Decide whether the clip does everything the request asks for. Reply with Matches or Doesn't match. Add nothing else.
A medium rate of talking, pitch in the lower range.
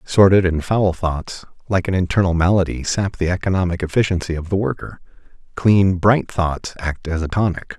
Matches